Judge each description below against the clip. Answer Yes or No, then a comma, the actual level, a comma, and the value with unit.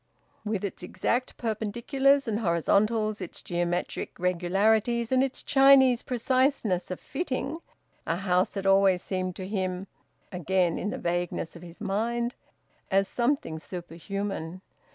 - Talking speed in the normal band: No, slow, 130 wpm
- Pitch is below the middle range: No, high, 200 Hz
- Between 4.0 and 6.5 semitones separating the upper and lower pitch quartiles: Yes, average, 4.7 semitones